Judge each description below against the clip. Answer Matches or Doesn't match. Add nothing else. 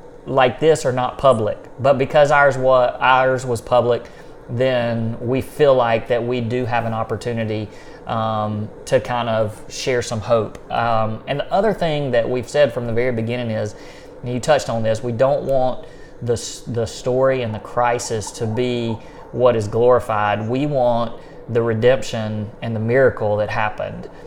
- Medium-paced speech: Matches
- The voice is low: Matches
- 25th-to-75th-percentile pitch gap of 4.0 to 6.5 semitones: Doesn't match